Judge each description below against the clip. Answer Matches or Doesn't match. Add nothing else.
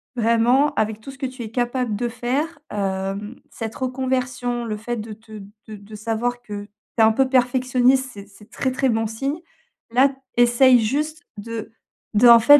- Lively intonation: Doesn't match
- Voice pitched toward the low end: Doesn't match